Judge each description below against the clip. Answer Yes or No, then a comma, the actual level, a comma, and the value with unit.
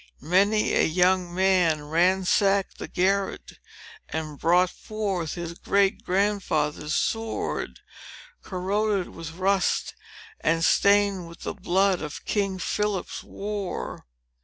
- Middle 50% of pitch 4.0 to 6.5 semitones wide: No, average, 2.9 semitones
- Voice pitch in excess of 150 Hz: Yes, medium, 185 Hz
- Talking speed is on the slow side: Yes, slow, 110 wpm